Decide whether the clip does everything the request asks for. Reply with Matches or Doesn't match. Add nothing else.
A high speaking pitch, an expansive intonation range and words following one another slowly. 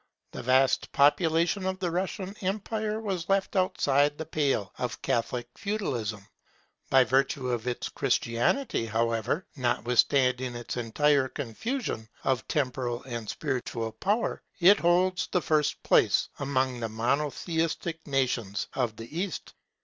Doesn't match